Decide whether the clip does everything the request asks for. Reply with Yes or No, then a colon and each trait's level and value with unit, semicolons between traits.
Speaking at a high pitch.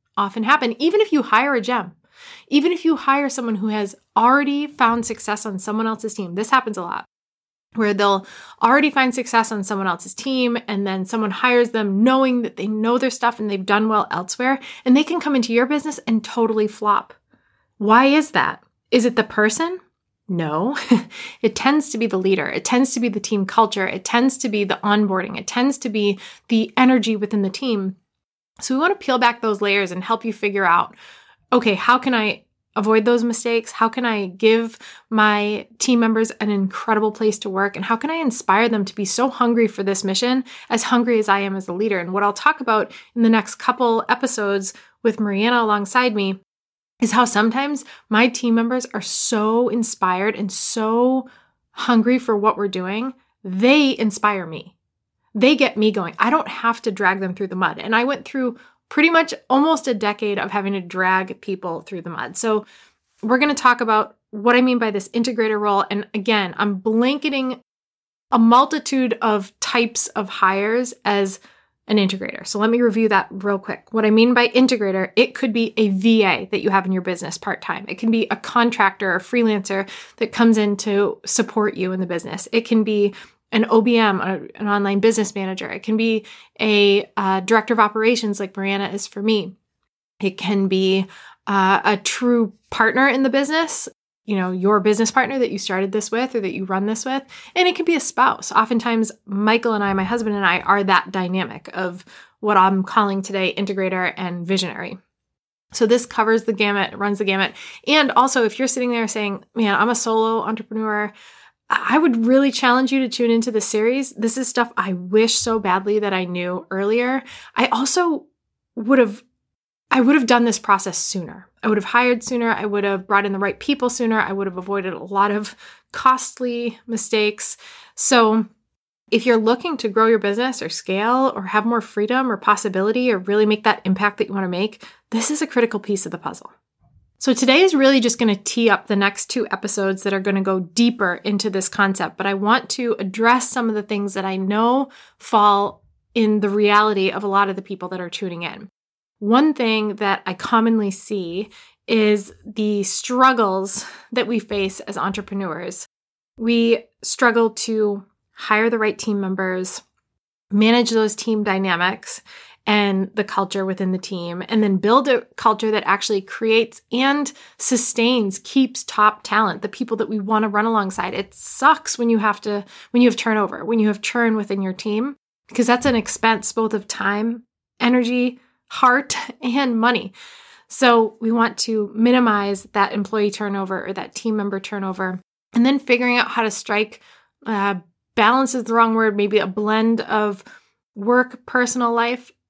Yes: high, 220 Hz